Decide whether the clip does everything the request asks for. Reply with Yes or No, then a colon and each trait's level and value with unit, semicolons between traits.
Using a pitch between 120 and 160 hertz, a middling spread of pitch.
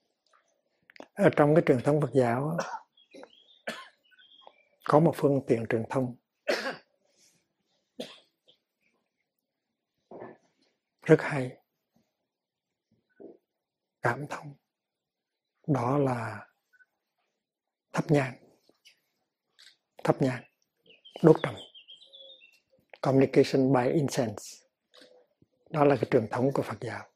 Yes: medium, 140 Hz; average, 3.7 semitones